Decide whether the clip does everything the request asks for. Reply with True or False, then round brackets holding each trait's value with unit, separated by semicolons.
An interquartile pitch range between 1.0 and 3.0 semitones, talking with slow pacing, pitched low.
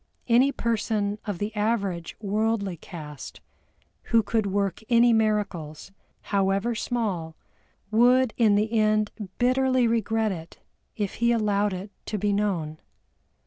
False (2.7 semitones; 125 wpm; 210 Hz)